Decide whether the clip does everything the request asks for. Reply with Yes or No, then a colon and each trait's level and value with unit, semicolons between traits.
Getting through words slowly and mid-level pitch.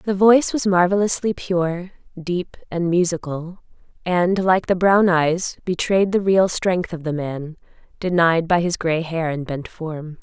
No: average, 165 wpm; medium, 175 Hz